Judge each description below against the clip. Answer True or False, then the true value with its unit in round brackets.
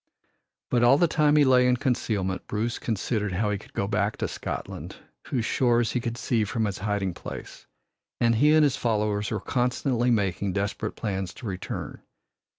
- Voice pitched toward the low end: True (110 Hz)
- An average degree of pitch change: True (3.5 semitones)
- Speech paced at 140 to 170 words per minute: False (180 wpm)